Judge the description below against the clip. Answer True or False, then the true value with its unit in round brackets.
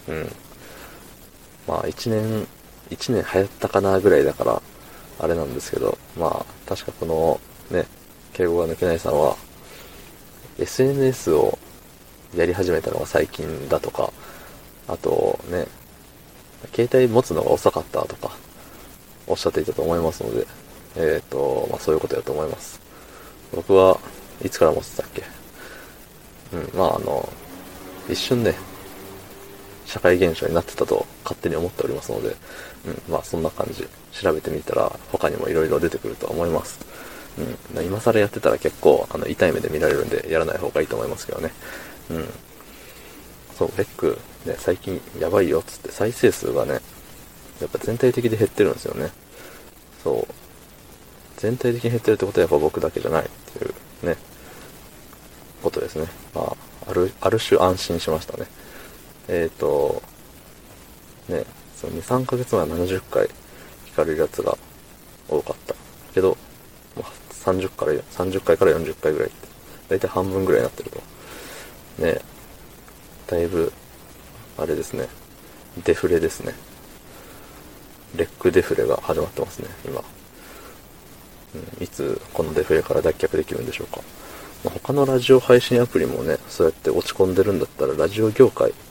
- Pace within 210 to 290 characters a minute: False (300 characters per minute)